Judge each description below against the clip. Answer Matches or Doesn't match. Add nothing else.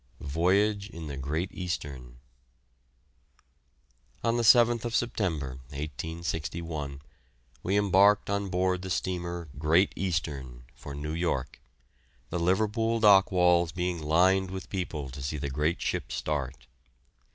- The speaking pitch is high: Doesn't match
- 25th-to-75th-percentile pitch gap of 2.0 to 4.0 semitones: Doesn't match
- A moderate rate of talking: Doesn't match